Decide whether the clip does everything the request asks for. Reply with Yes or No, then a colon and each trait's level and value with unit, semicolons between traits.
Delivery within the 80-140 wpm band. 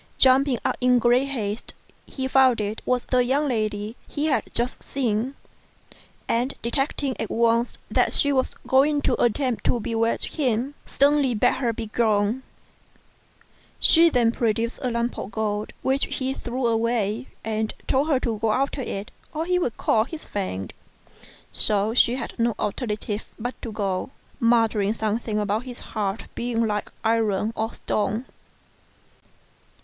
No: average, 150 wpm